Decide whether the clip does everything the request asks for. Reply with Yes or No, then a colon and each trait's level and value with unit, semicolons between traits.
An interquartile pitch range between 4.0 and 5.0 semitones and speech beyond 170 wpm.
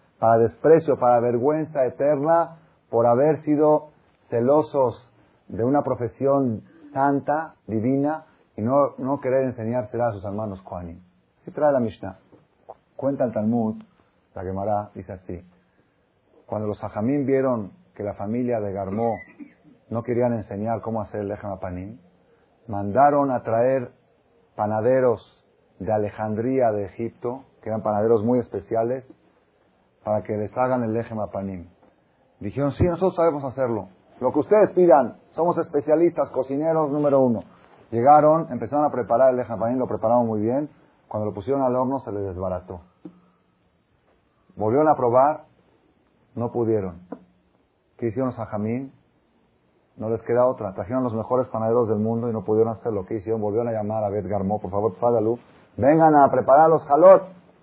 No: average, 4.4 semitones; average, 145 wpm